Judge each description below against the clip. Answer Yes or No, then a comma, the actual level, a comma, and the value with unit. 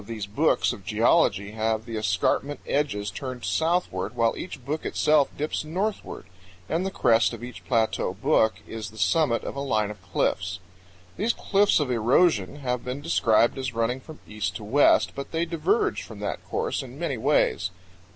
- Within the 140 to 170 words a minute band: No, average, 180 wpm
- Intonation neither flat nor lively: No, wide, 6.0 semitones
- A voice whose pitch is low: Yes, low, 125 Hz